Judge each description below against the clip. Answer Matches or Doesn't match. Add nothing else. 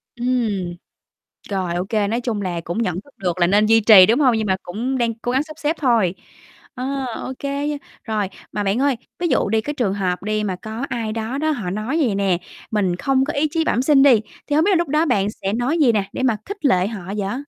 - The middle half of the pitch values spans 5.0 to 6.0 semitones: Matches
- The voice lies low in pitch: Doesn't match